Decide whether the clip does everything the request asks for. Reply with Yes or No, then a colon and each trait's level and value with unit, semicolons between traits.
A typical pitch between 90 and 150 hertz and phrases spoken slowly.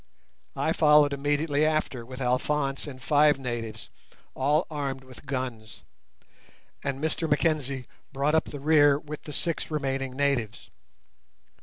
Yes: medium, 140 Hz; slow, 130 wpm